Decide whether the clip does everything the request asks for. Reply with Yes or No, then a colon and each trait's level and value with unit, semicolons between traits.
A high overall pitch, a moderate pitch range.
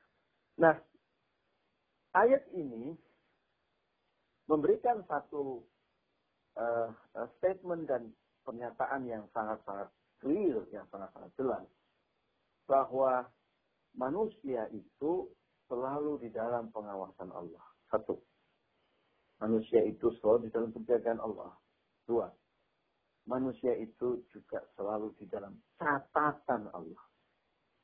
No: low, 120 Hz; average, 3.6 semitones